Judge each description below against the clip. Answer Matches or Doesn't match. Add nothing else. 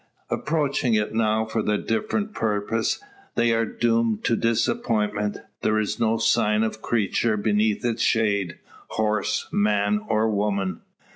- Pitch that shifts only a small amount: Matches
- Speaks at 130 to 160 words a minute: Matches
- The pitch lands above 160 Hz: Doesn't match